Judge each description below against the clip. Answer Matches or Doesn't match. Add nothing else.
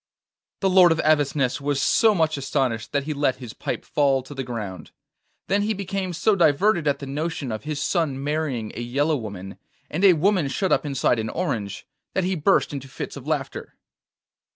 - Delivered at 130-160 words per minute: Doesn't match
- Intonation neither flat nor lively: Matches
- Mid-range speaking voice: Matches